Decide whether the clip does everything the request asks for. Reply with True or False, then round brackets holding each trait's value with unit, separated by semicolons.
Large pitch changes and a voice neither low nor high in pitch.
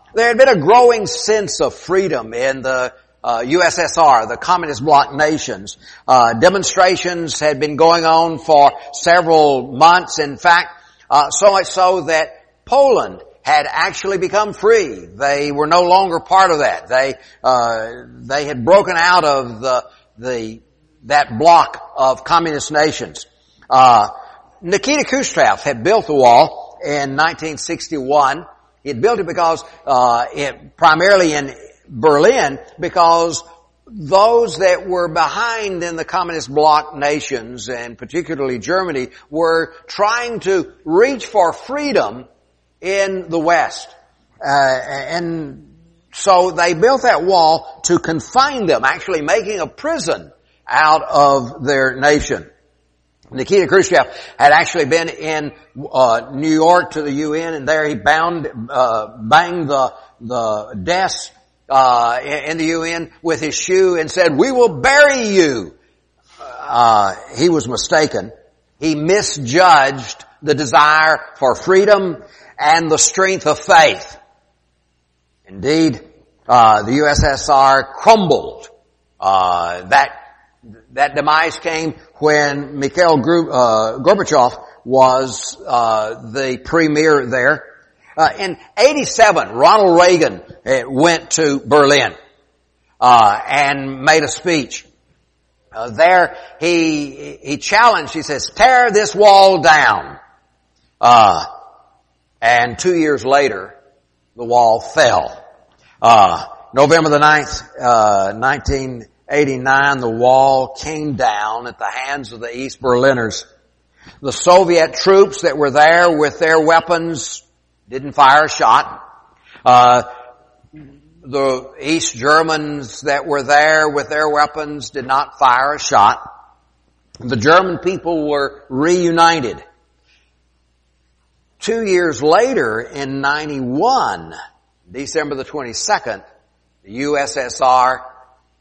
False (4.9 semitones; 155 Hz)